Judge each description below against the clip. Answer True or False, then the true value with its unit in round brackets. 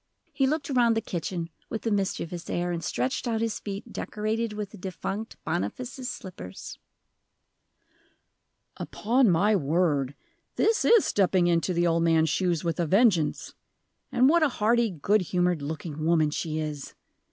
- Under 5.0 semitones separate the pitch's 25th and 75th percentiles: False (5.4 semitones)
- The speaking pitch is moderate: True (180 Hz)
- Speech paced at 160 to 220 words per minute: False (150 wpm)